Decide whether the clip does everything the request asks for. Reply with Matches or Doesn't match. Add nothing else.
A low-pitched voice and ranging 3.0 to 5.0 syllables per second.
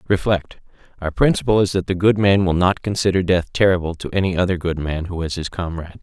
Doesn't match